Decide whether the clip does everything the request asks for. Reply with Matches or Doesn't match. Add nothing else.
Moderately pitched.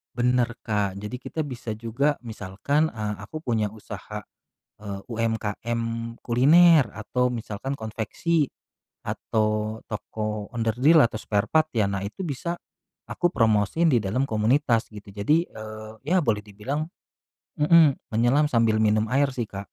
Doesn't match